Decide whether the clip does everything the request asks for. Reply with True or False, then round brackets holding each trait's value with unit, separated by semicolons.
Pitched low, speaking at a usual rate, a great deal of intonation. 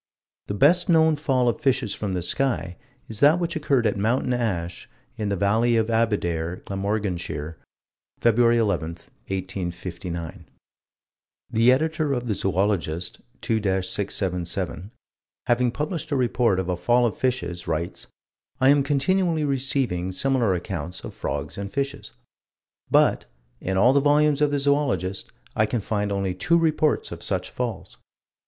True (110 Hz; 145 wpm; 6.7 semitones)